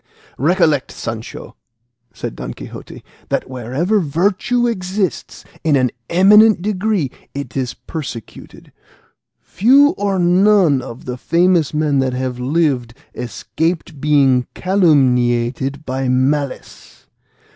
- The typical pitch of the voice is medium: Yes, medium, 150 Hz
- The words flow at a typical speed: No, slow, 105 wpm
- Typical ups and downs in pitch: No, wide, 6.3 semitones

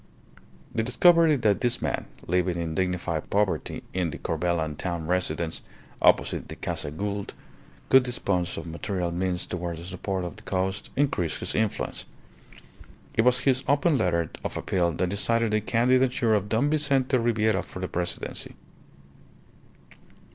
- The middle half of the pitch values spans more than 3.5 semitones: Yes, wide, 5.4 semitones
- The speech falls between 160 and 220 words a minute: No, average, 145 wpm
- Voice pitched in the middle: No, very low, 95 Hz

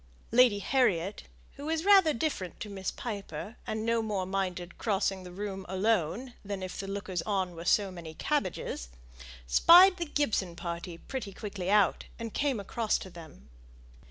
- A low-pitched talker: No, high, 200 Hz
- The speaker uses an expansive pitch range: No, average, 4.1 semitones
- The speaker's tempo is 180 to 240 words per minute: No, average, 160 wpm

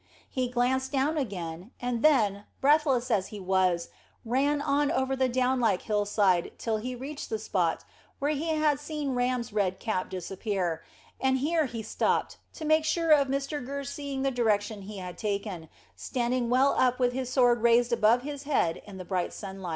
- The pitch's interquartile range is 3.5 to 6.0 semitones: Yes, average, 5.2 semitones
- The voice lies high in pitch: Yes, high, 245 Hz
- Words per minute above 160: Yes, average, 180 wpm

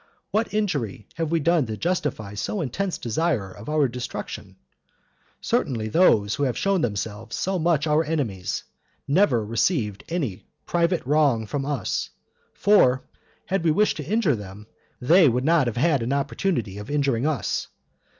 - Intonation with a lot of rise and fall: Yes, wide, 6.8 semitones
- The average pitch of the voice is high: No, medium, 140 Hz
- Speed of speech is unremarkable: Yes, average, 155 wpm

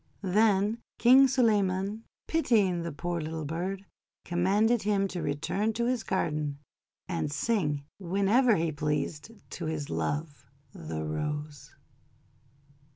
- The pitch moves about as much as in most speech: No, wide, 5.9 semitones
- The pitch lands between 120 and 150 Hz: No, medium, 180 Hz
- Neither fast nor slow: No, slow, 115 wpm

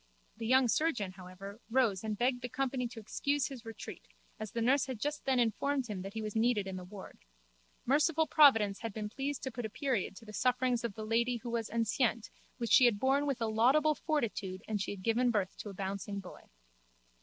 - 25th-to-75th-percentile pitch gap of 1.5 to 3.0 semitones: No, average, 3.9 semitones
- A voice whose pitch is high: Yes, high, 230 Hz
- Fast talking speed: Yes, fast, 220 wpm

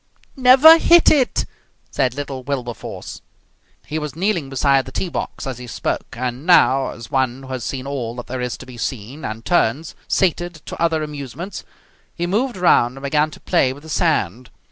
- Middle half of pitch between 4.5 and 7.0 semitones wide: Yes, average, 4.9 semitones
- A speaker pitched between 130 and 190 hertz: Yes, medium, 140 Hz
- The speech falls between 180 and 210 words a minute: Yes, average, 190 wpm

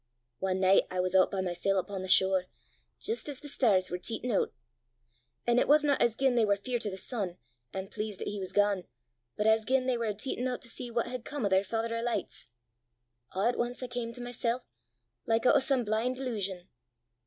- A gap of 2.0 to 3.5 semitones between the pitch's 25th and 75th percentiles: No, average, 4.3 semitones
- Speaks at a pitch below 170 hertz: No, high, 225 Hz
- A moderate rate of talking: No, fast, 225 wpm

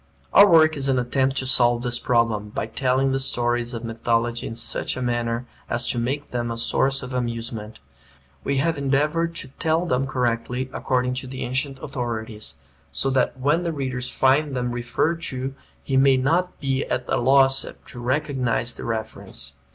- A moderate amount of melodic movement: No, narrow, 2.3 semitones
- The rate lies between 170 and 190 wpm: Yes, average, 180 wpm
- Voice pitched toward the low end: Yes, low, 130 Hz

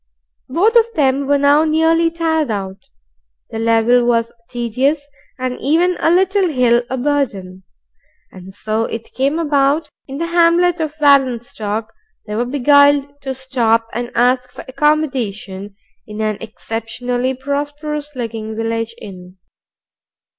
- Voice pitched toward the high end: Yes, very high, 260 Hz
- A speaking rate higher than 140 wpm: No, slow, 135 wpm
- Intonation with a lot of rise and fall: No, average, 4.6 semitones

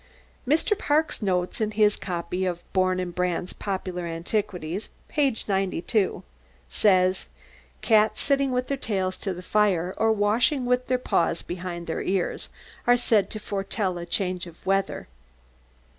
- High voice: Yes, high, 195 Hz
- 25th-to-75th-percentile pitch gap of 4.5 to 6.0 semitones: No, average, 3.5 semitones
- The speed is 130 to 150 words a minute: Yes, average, 145 wpm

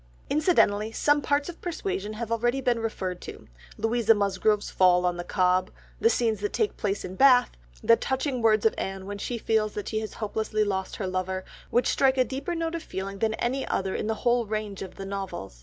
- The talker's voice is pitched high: Yes, high, 215 Hz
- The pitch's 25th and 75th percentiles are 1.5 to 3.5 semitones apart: No, average, 4.1 semitones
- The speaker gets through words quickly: Yes, fast, 210 wpm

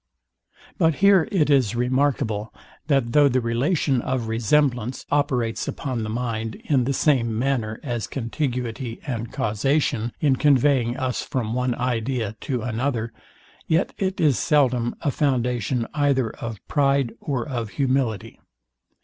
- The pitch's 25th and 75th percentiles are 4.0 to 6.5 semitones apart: No, average, 3.4 semitones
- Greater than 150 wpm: No, slow, 135 wpm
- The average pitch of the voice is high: No, low, 125 Hz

